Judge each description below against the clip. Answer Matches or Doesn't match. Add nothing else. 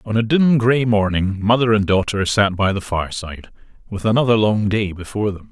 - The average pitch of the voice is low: Matches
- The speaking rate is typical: Matches